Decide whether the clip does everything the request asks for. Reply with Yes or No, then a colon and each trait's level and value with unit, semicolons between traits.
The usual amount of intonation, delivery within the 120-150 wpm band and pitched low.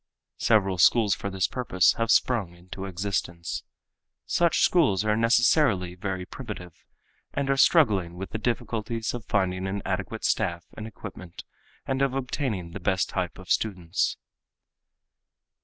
Yes: average, 4.0 semitones; average, 140 wpm; low, 100 Hz